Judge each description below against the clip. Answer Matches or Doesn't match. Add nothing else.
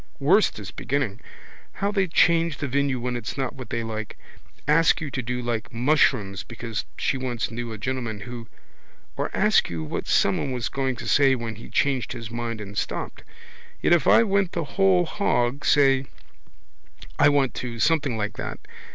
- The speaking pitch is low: Matches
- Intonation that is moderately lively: Matches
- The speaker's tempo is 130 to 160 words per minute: Doesn't match